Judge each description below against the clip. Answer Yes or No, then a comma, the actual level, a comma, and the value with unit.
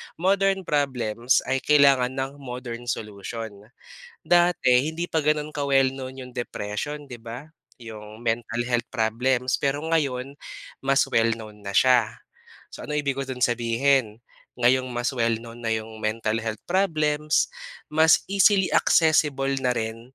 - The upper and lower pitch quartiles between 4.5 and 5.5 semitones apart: No, average, 4.1 semitones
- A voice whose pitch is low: Yes, low, 130 Hz